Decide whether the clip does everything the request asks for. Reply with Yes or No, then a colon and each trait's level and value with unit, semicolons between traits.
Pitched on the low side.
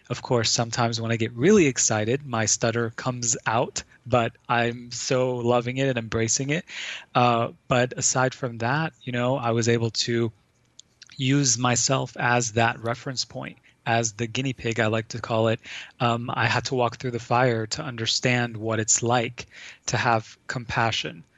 Yes: low, 120 Hz